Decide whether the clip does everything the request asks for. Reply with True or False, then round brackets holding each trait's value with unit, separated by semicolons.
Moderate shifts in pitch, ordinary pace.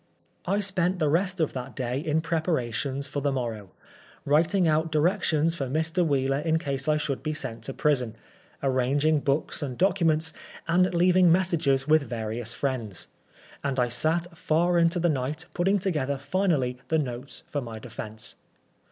True (4.3 semitones; 165 wpm)